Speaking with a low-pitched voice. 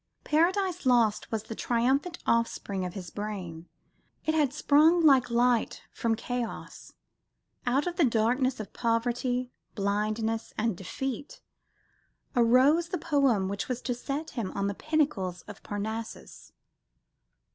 No: high, 240 Hz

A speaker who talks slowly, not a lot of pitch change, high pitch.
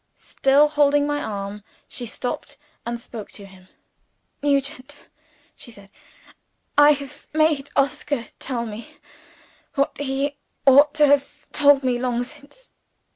No: slow, 130 wpm; average, 3.3 semitones; very high, 275 Hz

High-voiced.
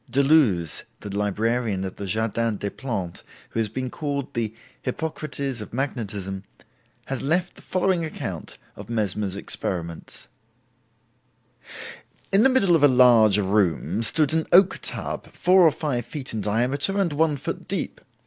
No: low, 120 Hz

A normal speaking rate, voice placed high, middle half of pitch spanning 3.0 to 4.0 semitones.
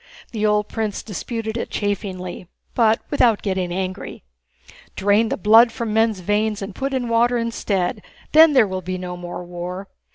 Yes: average, 165 wpm; high, 210 Hz; average, 3.6 semitones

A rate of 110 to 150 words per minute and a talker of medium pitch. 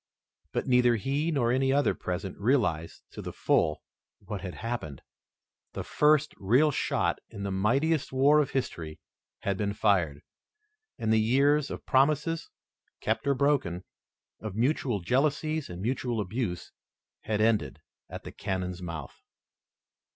No: average, 140 wpm; low, 115 Hz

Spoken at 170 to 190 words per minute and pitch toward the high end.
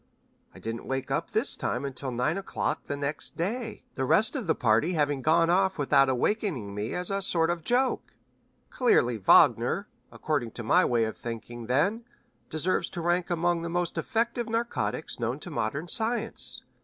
No: average, 175 wpm; medium, 165 Hz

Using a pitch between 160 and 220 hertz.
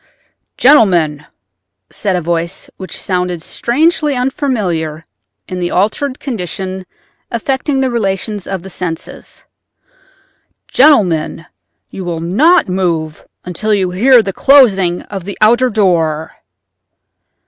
Yes: high, 190 Hz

